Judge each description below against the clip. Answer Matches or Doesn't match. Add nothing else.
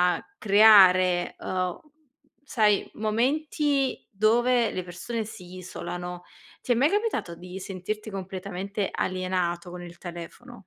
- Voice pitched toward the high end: Matches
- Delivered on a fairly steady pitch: Doesn't match